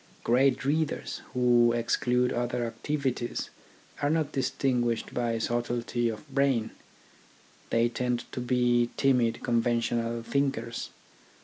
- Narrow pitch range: Yes, narrow, 1.9 semitones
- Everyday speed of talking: No, slow, 105 wpm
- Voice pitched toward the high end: No, low, 120 Hz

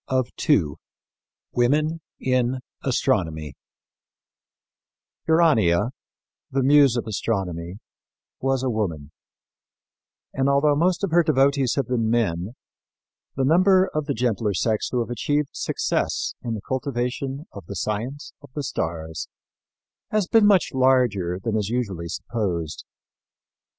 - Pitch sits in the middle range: No, low, 125 Hz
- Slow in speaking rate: Yes, slow, 125 wpm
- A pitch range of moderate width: No, wide, 5.7 semitones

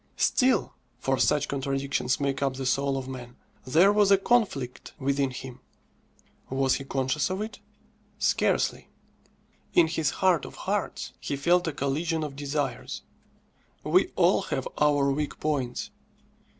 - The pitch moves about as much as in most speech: Yes, average, 3.3 semitones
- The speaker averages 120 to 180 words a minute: Yes, average, 140 wpm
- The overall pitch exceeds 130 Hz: Yes, medium, 140 Hz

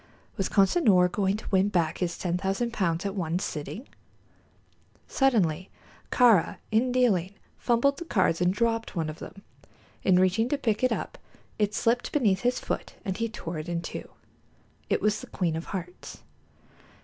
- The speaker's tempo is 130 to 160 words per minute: No, average, 170 wpm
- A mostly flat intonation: No, average, 4.5 semitones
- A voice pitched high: Yes, high, 195 Hz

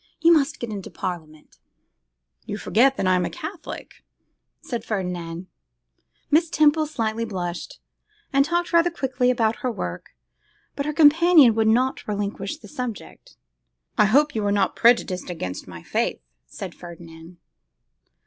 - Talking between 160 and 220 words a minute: No, average, 145 wpm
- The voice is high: Yes, high, 225 Hz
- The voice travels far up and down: Yes, wide, 8.0 semitones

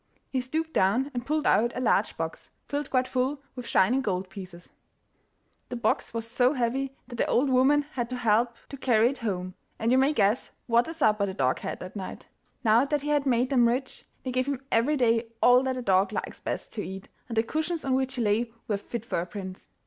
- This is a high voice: Yes, high, 245 Hz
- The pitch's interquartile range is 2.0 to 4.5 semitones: Yes, average, 3.8 semitones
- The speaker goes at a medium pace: No, fast, 230 wpm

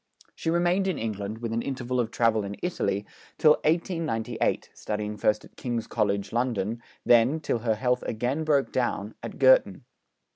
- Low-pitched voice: Yes, low, 120 Hz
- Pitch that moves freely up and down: Yes, wide, 5.7 semitones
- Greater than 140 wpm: Yes, average, 160 wpm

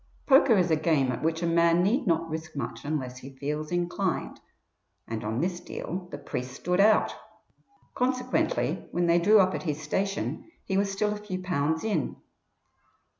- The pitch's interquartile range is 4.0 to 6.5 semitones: Yes, average, 4.3 semitones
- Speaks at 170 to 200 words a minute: Yes, average, 175 wpm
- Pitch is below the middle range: No, medium, 175 Hz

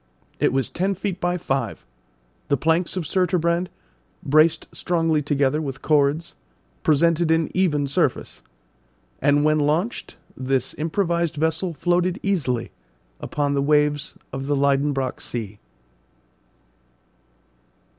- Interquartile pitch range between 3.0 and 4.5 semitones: Yes, average, 3.4 semitones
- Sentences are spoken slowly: Yes, slow, 115 wpm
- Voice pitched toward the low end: No, medium, 155 Hz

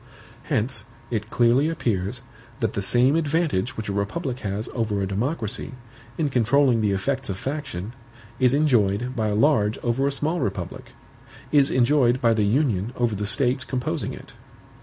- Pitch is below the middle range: Yes, low, 120 Hz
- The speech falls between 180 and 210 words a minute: No, average, 160 wpm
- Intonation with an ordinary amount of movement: Yes, average, 4.7 semitones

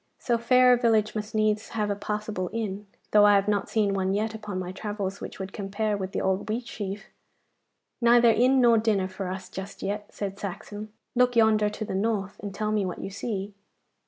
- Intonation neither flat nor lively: No, narrow, 2.0 semitones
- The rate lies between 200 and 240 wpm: Yes, fast, 205 wpm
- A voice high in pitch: Yes, high, 210 Hz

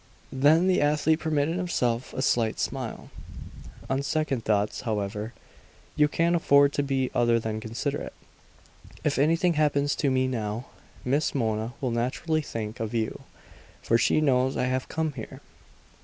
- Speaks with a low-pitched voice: Yes, low, 130 Hz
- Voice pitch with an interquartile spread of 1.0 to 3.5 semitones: No, average, 4.6 semitones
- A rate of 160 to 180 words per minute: No, average, 150 wpm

